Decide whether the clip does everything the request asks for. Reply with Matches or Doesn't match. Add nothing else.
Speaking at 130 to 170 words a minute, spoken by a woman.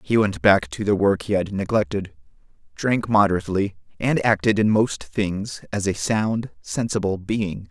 Doesn't match